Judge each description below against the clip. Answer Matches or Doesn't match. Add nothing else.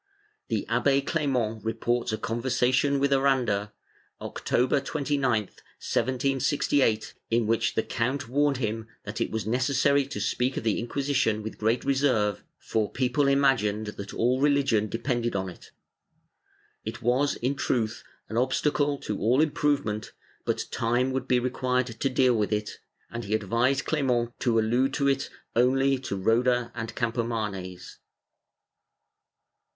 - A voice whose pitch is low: Matches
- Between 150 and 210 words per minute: Doesn't match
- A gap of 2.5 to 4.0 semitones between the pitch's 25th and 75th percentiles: Matches